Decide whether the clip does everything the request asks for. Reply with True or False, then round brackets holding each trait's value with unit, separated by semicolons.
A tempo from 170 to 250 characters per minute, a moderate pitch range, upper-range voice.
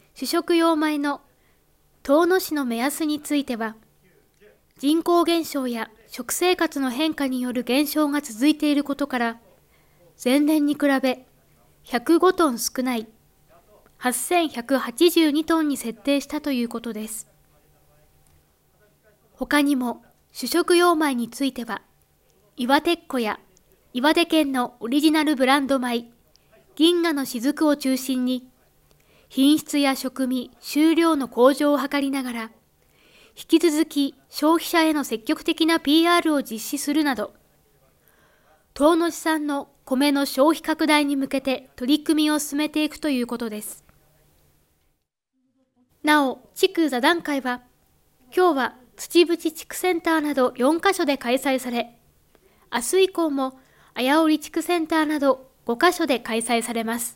True (240 characters per minute; 4.0 semitones; 285 Hz)